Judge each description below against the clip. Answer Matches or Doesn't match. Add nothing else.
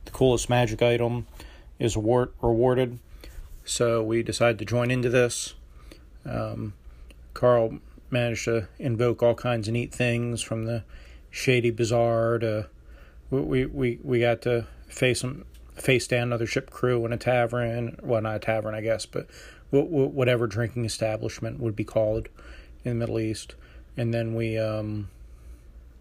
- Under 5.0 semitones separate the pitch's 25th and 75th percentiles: Matches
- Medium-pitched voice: Doesn't match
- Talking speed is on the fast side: Doesn't match